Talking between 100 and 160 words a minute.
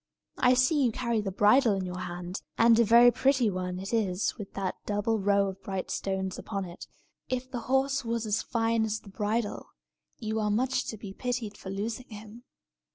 No: average, 200 wpm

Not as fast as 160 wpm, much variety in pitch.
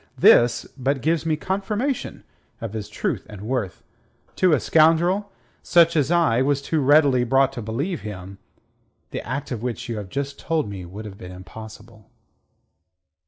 No: average, 165 wpm; wide, 6.6 semitones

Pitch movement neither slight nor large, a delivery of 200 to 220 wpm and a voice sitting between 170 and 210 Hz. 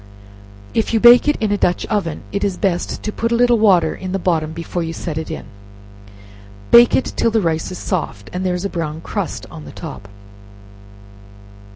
Yes: average, 4.9 semitones; fast, 205 wpm; medium, 185 Hz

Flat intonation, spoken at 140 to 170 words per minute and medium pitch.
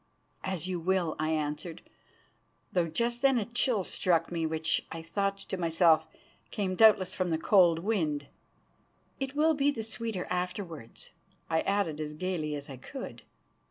No: average, 4.2 semitones; average, 160 wpm; medium, 180 Hz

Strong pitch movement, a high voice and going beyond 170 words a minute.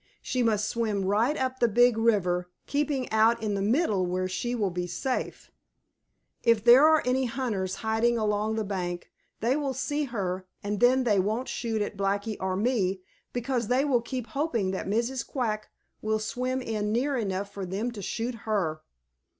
No: average, 3.8 semitones; high, 220 Hz; average, 180 wpm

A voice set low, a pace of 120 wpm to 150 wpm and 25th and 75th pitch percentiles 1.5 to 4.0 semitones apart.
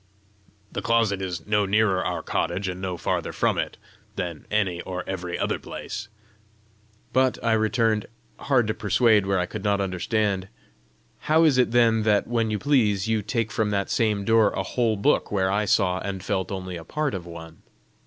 No: low, 105 Hz; average, 185 wpm; average, 3.1 semitones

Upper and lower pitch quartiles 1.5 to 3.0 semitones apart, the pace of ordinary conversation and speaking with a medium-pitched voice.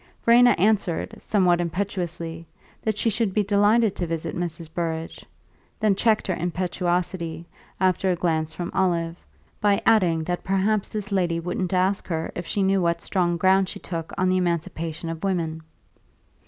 Yes: average, 2.7 semitones; average, 160 wpm; medium, 180 Hz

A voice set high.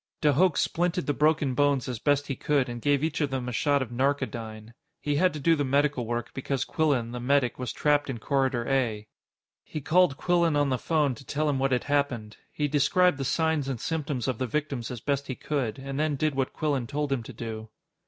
No: medium, 140 Hz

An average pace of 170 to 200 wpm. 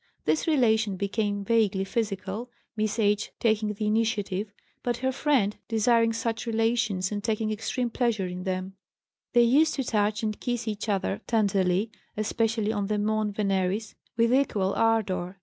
No: average, 150 wpm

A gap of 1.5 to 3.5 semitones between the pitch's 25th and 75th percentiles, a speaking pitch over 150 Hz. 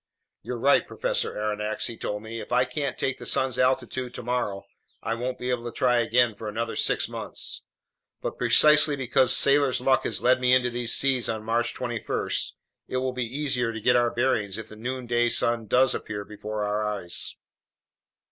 No: narrow, 2.5 semitones; low, 120 Hz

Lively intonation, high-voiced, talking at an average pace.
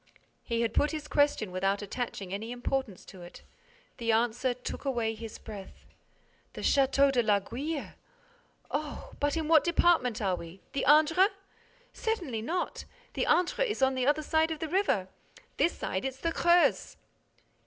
Yes: wide, 6.2 semitones; very high, 265 Hz; average, 155 wpm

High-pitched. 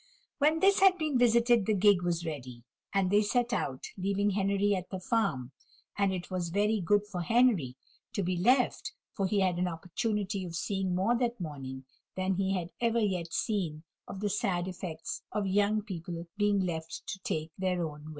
Yes: high, 195 Hz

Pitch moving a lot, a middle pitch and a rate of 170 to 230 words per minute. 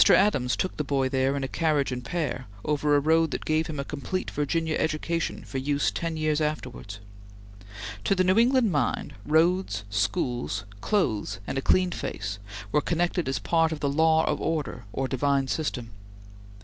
No: average, 3.6 semitones; medium, 150 Hz; average, 175 wpm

